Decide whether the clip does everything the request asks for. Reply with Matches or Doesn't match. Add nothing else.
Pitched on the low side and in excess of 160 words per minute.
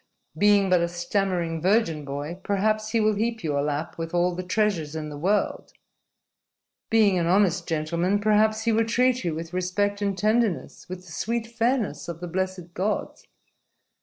Doesn't match